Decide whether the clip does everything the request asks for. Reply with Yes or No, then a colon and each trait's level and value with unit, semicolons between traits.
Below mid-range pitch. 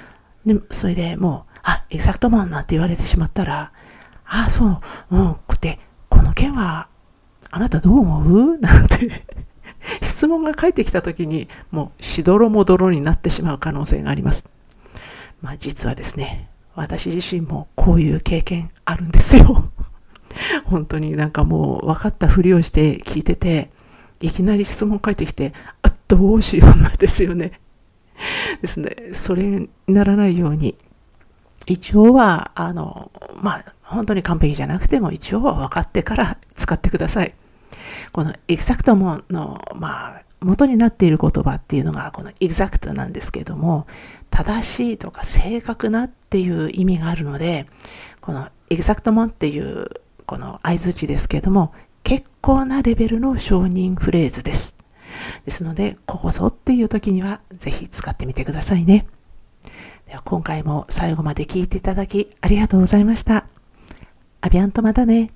No: medium, 185 Hz